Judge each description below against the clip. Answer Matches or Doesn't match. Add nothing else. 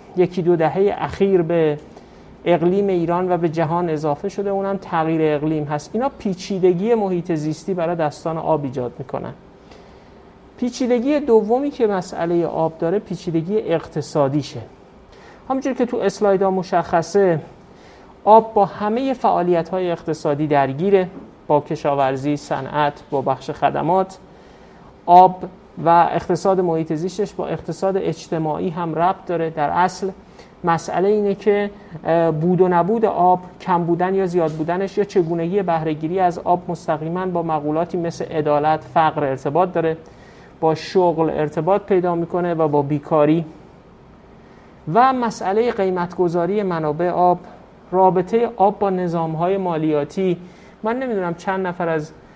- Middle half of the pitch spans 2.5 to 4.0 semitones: Matches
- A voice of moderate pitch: Matches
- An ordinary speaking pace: Matches